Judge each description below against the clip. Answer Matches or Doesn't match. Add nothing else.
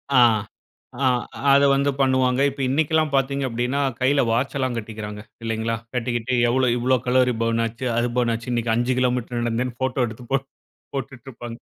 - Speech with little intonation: Matches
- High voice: Doesn't match